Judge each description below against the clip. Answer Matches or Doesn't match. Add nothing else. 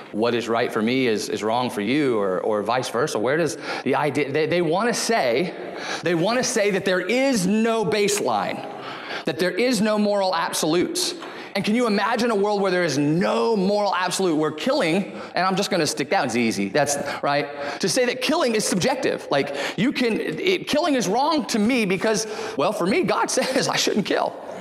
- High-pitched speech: Matches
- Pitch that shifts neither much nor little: Doesn't match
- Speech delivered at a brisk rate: Matches